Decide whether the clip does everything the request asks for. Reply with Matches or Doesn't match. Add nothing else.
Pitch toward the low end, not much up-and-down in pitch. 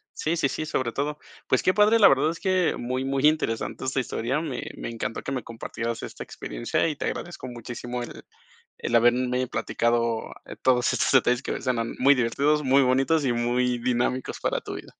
Doesn't match